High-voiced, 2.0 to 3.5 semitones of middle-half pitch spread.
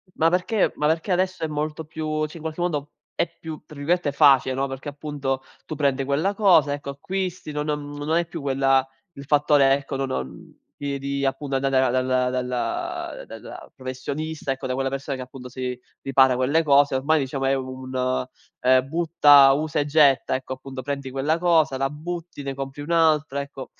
No: medium, 140 Hz; average, 2.7 semitones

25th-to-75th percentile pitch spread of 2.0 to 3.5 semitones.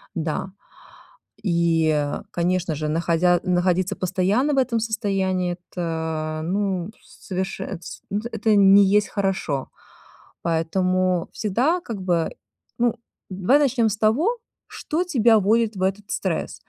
No: average, 4.0 semitones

